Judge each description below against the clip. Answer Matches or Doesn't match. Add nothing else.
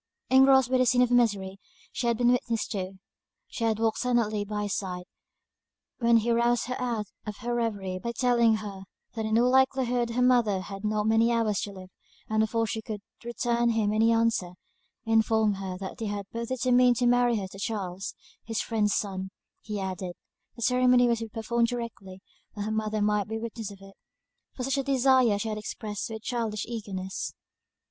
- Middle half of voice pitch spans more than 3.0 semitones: Doesn't match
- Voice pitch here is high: Matches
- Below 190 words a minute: Doesn't match